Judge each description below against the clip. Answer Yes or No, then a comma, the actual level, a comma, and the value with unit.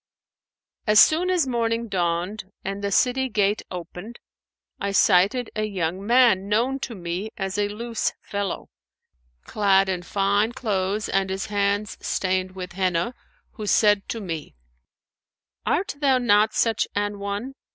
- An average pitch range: Yes, average, 3.2 semitones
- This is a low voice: No, high, 205 Hz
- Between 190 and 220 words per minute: No, average, 140 wpm